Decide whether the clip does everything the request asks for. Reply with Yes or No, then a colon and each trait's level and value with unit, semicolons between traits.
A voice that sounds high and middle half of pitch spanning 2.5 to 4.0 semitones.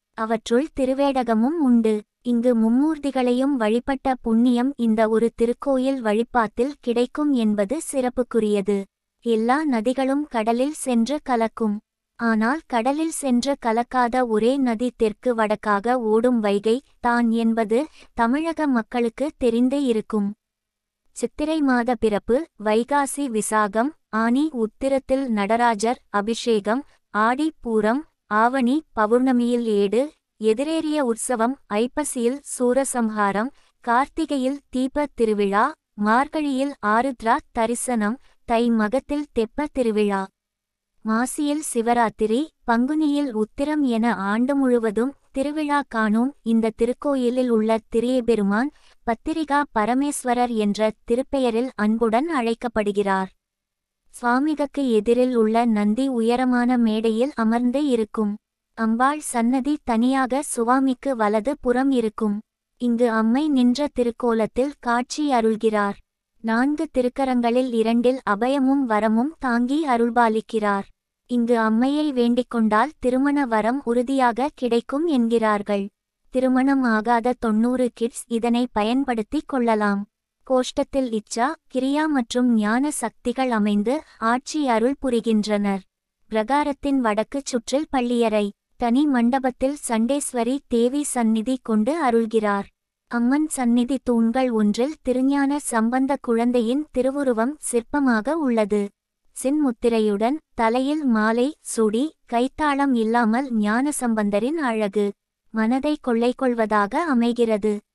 Yes: high, 240 Hz; average, 3.1 semitones